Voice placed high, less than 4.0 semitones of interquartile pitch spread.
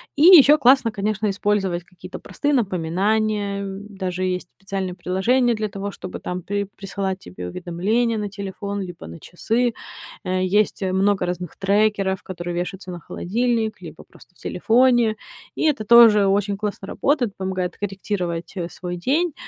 Yes: high, 200 Hz; average, 2.9 semitones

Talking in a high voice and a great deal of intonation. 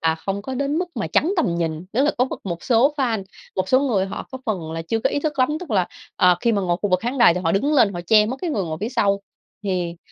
Yes: high, 210 Hz; wide, 6.4 semitones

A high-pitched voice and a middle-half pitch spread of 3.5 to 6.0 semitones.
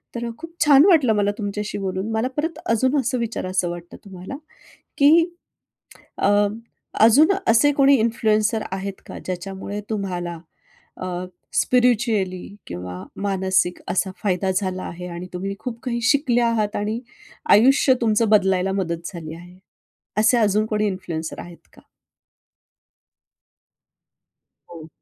Yes: high, 205 Hz; average, 4.2 semitones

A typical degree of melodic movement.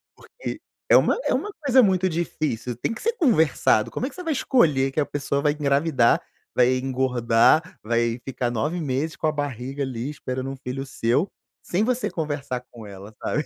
Yes: average, 4.9 semitones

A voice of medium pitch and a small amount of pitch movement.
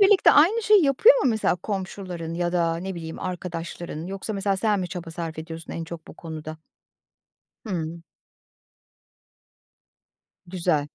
No: medium, 175 Hz; average, 3.3 semitones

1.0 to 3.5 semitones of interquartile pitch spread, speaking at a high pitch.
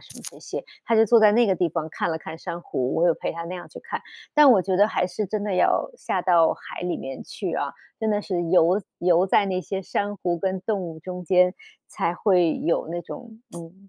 No: average, 3.1 semitones; medium, 180 Hz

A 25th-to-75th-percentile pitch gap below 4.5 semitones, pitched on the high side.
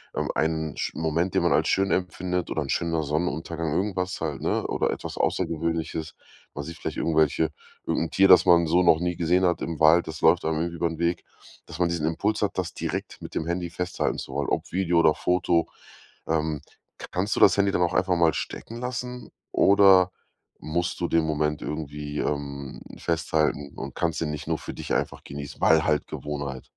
No: narrow, 2.5 semitones; very low, 85 Hz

